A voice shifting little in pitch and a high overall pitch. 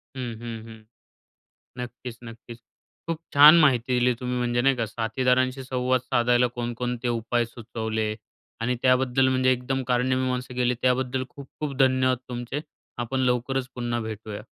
No: narrow, 1.5 semitones; low, 125 Hz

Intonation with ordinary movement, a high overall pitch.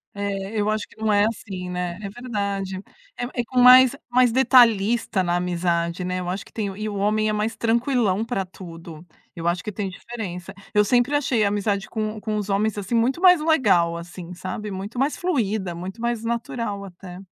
Yes: average, 3.9 semitones; high, 210 Hz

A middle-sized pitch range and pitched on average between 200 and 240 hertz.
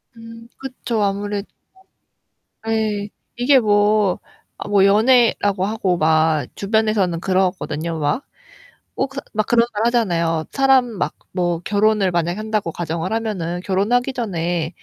Yes: average, 4.3 semitones; high, 205 Hz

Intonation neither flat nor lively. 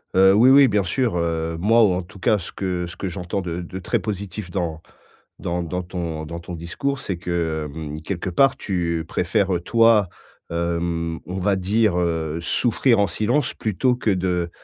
Yes: average, 3.4 semitones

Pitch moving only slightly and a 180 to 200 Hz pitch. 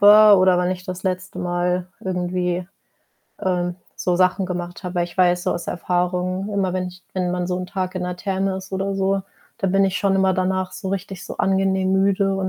Yes: narrow, 1.1 semitones; medium, 185 Hz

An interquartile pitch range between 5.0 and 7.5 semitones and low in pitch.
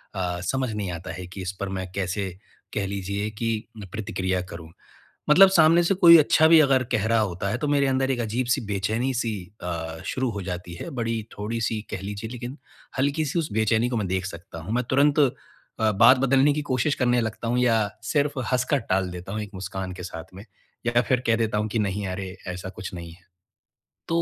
Yes: wide, 5.4 semitones; low, 110 Hz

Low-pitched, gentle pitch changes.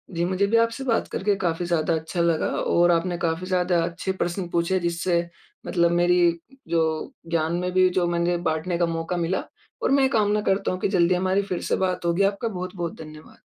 No: medium, 175 Hz; narrow, 1.7 semitones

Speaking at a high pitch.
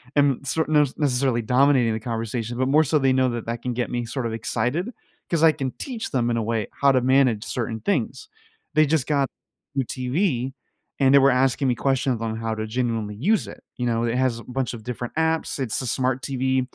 No: low, 130 Hz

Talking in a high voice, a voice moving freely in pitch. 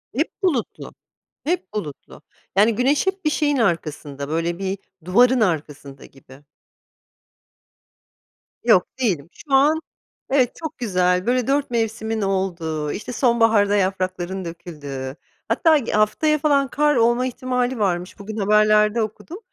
Yes: high, 215 Hz; wide, 6.2 semitones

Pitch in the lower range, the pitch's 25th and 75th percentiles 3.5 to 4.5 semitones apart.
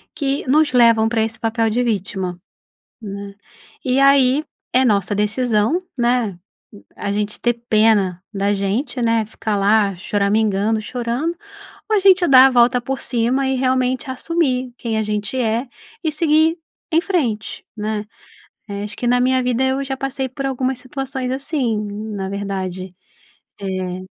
No: high, 235 Hz; average, 4.2 semitones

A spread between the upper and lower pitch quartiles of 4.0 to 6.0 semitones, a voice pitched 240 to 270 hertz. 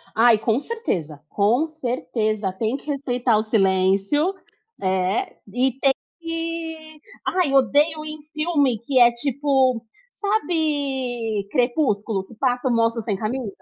Yes: wide, 5.6 semitones; very high, 250 Hz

